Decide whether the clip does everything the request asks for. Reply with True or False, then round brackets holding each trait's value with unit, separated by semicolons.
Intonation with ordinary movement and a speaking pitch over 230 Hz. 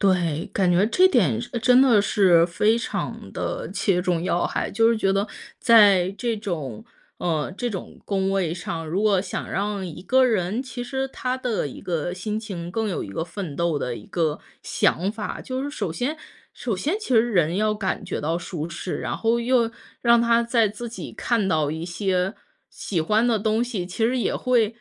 False (5.0 semitones; 200 Hz)